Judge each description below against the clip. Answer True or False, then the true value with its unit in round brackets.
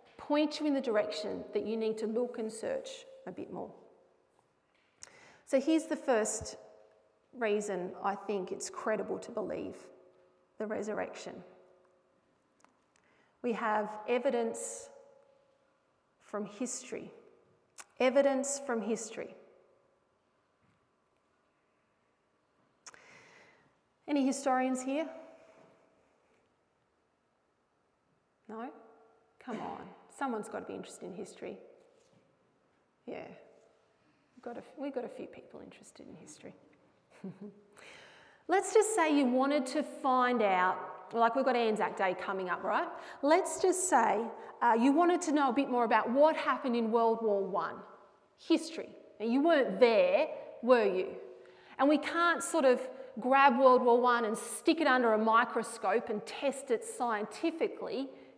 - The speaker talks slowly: True (125 wpm)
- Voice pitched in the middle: False (260 Hz)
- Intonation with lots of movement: True (5.8 semitones)